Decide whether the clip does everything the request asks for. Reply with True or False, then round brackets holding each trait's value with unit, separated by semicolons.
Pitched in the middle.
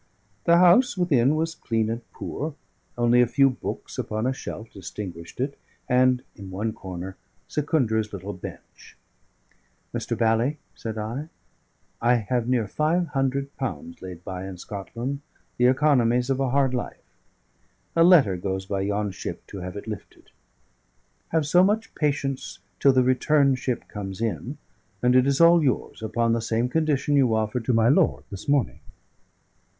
False (125 Hz)